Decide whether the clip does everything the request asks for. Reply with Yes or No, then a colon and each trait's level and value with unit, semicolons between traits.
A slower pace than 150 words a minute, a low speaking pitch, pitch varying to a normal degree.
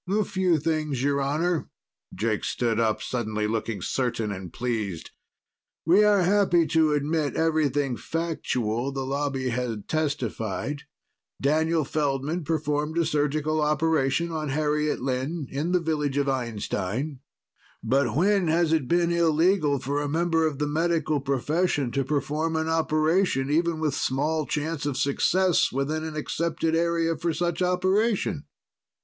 No: average, 140 wpm; medium, 150 Hz; average, 3.4 semitones